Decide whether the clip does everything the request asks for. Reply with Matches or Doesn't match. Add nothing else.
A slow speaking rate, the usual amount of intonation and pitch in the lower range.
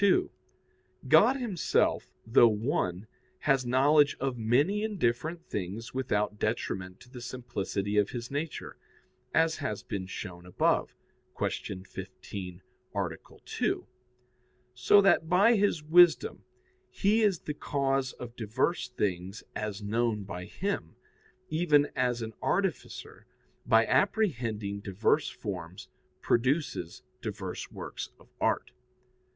Doesn't match